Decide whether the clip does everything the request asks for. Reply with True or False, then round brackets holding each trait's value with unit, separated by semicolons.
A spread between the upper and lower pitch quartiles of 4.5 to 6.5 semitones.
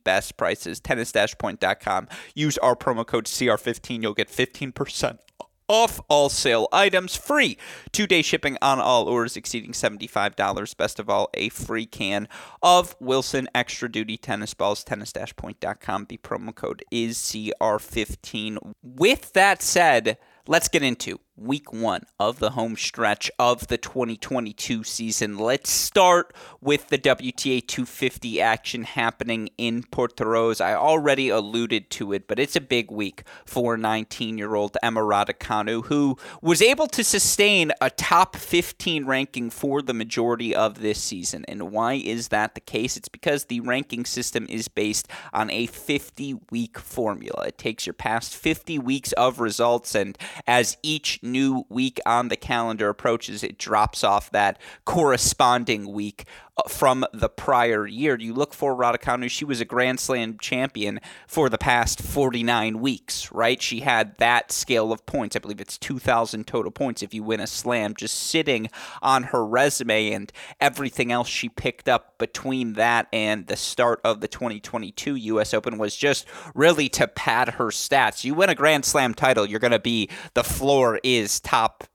False (3.7 semitones)